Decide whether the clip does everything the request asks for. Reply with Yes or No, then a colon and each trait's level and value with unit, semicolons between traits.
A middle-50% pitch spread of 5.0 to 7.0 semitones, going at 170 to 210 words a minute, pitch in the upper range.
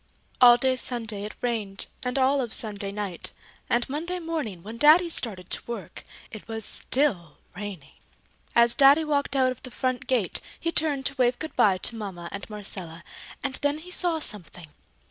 Yes: wide, 5.6 semitones; average, 180 wpm; high, 240 Hz